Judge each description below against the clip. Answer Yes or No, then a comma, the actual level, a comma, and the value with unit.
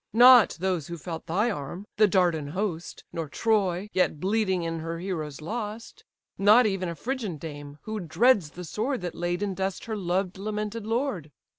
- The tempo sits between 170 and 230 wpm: Yes, average, 175 wpm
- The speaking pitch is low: No, high, 190 Hz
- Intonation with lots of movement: No, average, 4.3 semitones